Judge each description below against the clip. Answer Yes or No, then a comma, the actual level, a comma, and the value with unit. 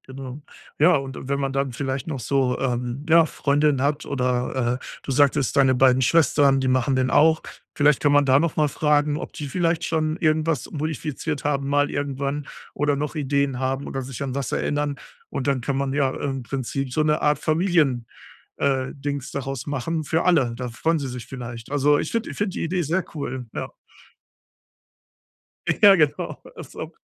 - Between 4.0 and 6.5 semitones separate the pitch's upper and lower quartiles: No, narrow, 2.4 semitones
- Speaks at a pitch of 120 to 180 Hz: Yes, medium, 140 Hz